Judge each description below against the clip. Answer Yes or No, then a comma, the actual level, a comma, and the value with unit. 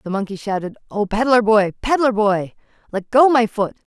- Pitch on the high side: Yes, high, 220 Hz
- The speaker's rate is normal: Yes, average, 180 wpm